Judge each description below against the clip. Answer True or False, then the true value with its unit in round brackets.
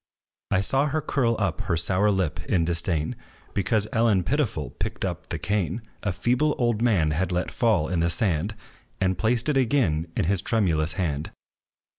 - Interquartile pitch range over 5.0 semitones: True (5.6 semitones)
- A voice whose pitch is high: False (95 Hz)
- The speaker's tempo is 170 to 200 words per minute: True (175 wpm)